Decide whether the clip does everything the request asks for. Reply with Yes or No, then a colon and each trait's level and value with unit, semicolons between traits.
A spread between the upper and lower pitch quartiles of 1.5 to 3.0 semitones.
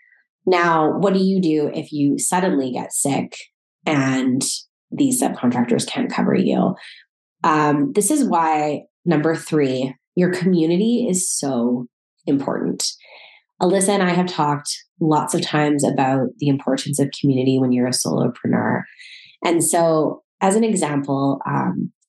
No: average, 4.6 semitones